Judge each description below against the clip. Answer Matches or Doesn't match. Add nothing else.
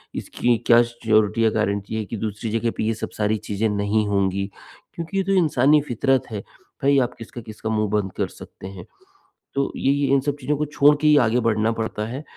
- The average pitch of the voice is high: Doesn't match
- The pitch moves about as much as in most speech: Matches